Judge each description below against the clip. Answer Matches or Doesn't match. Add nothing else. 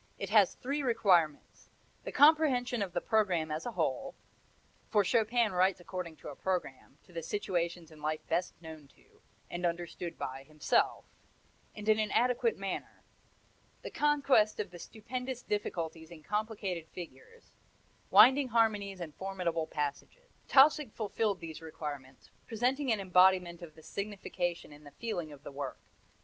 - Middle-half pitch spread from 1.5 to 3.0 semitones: Doesn't match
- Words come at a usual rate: Matches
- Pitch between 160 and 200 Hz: Matches